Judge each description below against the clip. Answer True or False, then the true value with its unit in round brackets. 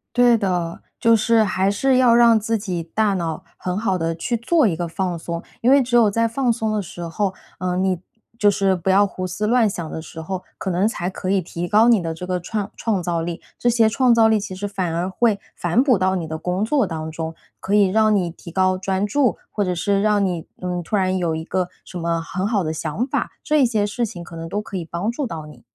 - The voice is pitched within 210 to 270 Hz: False (190 Hz)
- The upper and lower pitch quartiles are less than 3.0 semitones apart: False (4.1 semitones)